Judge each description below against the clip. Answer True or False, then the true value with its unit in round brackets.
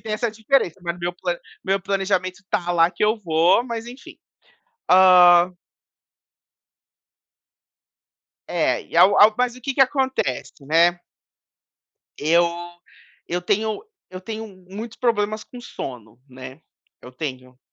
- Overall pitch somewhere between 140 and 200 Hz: True (185 Hz)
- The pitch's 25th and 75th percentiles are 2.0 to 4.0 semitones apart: False (4.4 semitones)